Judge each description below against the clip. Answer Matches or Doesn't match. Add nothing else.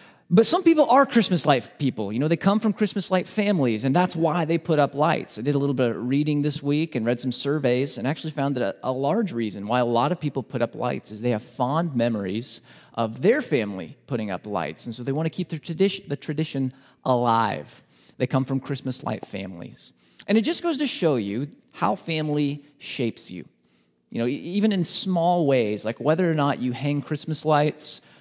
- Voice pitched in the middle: Matches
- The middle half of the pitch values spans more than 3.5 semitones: Matches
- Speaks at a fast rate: Matches